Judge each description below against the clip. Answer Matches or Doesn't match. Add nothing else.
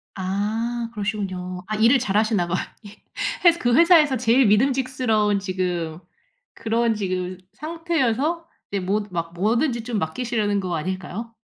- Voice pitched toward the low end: Doesn't match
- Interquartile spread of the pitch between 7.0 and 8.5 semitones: Doesn't match